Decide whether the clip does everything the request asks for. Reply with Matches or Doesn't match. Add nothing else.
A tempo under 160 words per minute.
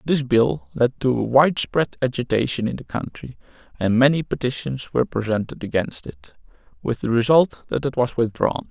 Doesn't match